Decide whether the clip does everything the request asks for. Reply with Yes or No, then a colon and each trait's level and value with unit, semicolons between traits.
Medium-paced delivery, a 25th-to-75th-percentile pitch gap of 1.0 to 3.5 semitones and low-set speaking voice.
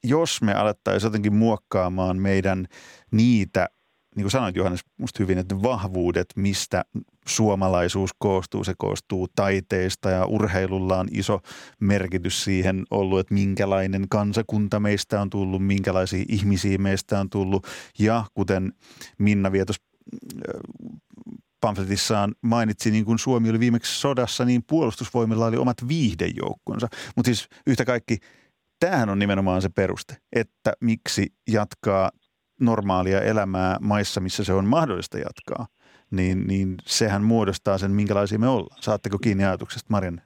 Yes: average, 135 wpm; average, 2.9 semitones; low, 100 Hz